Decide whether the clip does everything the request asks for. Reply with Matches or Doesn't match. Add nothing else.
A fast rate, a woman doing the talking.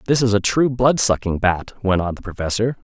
Doesn't match